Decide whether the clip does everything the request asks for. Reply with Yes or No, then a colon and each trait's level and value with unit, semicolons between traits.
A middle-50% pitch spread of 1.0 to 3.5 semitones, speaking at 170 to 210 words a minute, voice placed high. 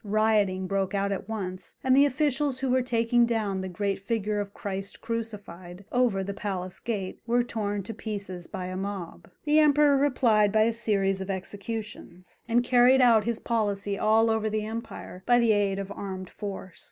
Yes: average, 3.1 semitones; average, 185 wpm; high, 210 Hz